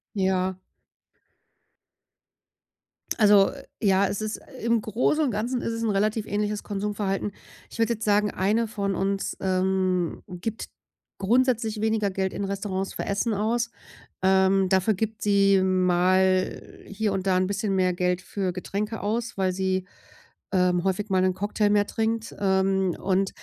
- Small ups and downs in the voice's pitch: Yes, narrow, 2.2 semitones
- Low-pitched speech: No, high, 200 Hz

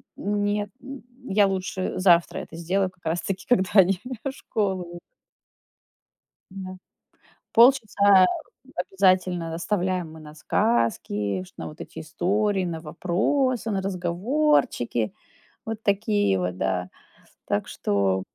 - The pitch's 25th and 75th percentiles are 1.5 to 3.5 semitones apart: No, average, 4.2 semitones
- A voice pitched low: No, medium, 185 Hz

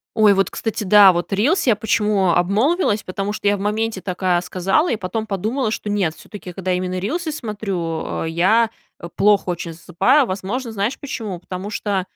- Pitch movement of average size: Yes, average, 3.1 semitones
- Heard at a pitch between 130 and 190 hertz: No, high, 200 Hz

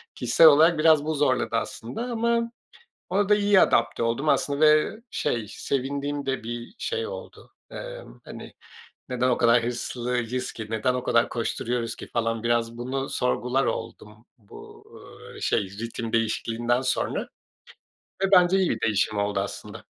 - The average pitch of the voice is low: Yes, low, 125 Hz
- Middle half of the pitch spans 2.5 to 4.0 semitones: No, average, 5.2 semitones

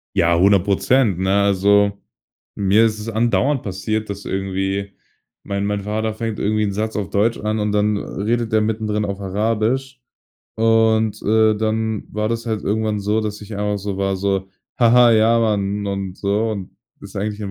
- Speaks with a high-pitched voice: No, low, 105 Hz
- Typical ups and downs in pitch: No, narrow, 1.8 semitones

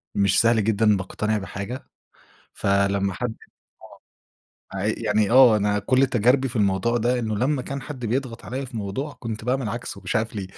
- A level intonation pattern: No, average, 3.6 semitones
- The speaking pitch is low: Yes, low, 110 Hz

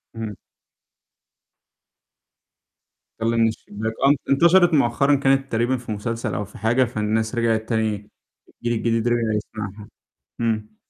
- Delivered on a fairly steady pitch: Yes, narrow, 1.9 semitones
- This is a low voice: Yes, low, 115 Hz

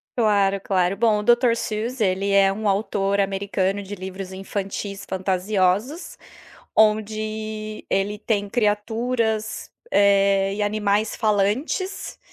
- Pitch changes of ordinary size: No, narrow, 1.8 semitones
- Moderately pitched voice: No, high, 205 Hz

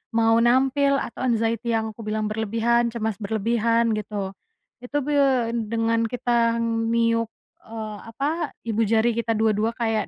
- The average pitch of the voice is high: Yes, high, 230 Hz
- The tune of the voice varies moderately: No, narrow, 1.2 semitones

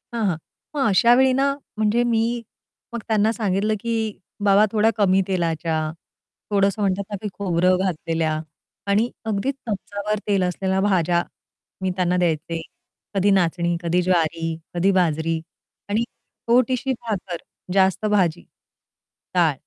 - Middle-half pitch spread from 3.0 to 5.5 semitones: Yes, average, 3.7 semitones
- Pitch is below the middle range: No, high, 195 Hz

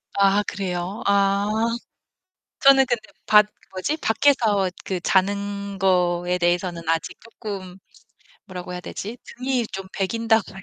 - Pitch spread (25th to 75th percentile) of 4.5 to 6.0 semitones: No, average, 3.1 semitones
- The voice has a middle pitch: No, high, 195 Hz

